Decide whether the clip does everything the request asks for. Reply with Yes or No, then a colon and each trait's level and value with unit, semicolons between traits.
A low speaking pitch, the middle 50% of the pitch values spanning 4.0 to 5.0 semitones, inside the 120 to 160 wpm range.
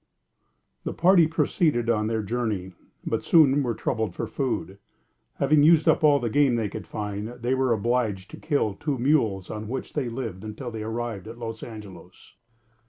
No: low, 115 Hz; average, 4.3 semitones; average, 175 wpm